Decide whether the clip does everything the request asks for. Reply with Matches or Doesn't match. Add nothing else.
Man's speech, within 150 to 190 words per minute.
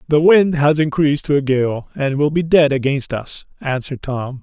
Doesn't match